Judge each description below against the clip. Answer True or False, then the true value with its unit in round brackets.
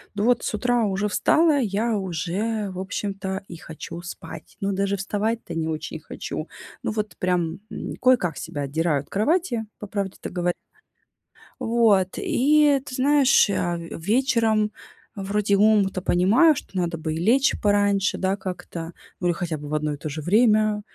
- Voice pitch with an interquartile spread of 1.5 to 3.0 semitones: False (4.2 semitones)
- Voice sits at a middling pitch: False (200 Hz)